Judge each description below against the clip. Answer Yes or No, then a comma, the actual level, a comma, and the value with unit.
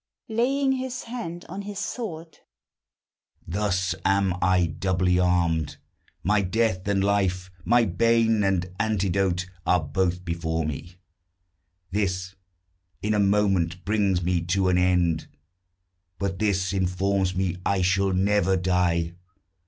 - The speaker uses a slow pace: Yes, slow, 120 wpm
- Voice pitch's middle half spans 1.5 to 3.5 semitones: Yes, narrow, 2.6 semitones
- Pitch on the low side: Yes, very low, 95 Hz